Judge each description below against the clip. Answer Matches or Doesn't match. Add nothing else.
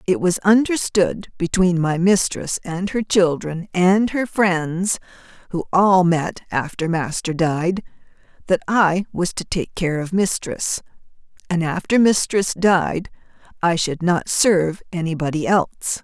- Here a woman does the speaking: Matches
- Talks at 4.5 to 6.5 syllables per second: Doesn't match